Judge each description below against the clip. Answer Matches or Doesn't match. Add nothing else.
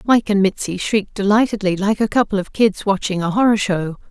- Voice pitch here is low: Doesn't match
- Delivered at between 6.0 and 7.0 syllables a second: Doesn't match